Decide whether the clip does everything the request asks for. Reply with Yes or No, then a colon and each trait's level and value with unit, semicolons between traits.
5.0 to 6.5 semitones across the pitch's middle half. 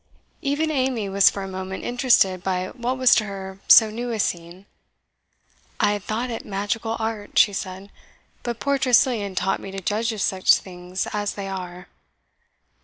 No: average, 3.7 semitones